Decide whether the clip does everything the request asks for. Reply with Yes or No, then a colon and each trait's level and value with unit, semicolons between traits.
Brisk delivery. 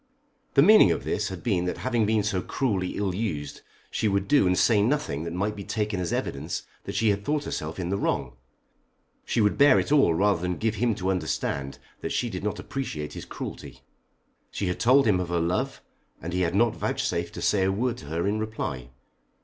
Yes: fast, 220 wpm